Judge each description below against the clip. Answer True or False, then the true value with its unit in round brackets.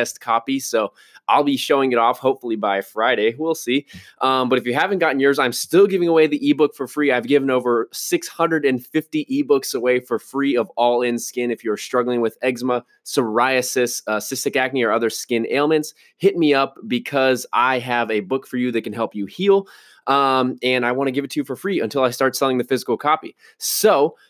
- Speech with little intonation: False (4.3 semitones)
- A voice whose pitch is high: False (130 Hz)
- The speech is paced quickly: True (215 wpm)